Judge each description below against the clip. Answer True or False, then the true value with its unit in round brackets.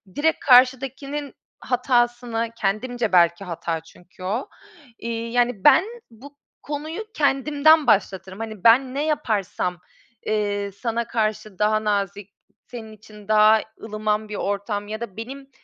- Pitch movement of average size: True (3.9 semitones)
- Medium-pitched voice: False (225 Hz)